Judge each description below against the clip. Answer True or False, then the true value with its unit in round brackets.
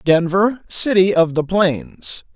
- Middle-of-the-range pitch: True (180 Hz)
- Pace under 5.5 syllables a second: True (3.3 syllables/s)